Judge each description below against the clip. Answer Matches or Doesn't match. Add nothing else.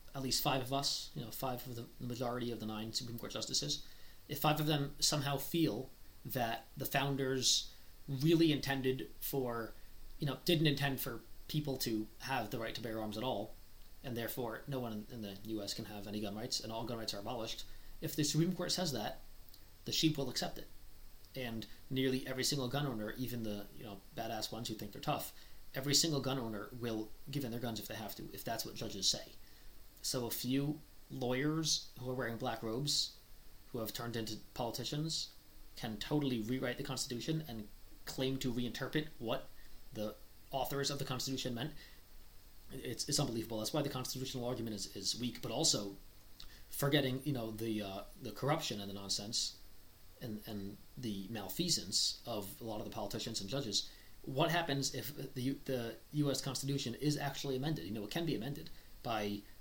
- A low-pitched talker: Matches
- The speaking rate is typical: Matches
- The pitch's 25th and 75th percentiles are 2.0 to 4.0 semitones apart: Doesn't match